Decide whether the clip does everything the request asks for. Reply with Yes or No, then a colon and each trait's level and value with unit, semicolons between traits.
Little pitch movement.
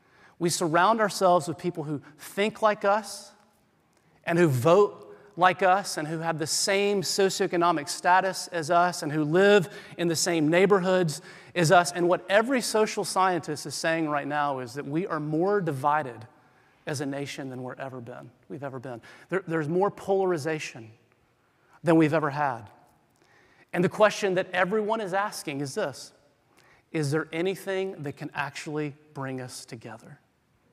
No: average, 4.7 semitones